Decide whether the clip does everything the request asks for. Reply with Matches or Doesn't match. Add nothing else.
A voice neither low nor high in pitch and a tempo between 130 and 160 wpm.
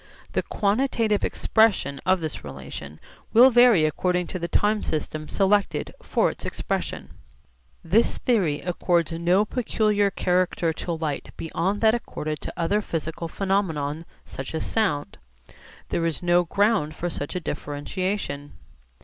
Matches